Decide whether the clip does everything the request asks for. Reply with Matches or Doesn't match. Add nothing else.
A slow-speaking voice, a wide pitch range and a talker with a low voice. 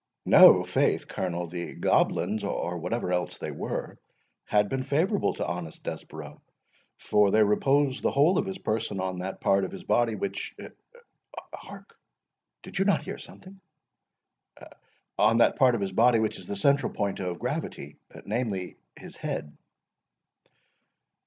Matches